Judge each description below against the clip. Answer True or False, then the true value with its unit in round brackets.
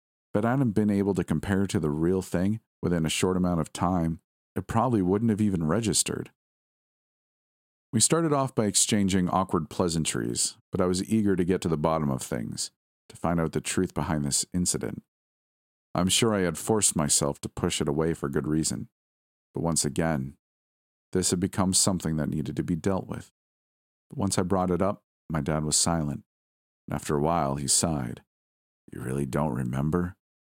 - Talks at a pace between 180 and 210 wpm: True (185 wpm)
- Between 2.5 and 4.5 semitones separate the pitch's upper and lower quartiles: False (5.0 semitones)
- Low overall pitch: True (85 Hz)